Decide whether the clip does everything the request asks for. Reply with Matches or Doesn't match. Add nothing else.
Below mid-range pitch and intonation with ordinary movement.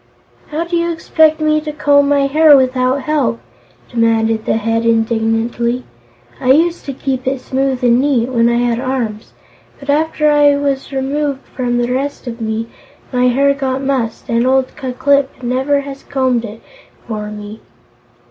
Doesn't match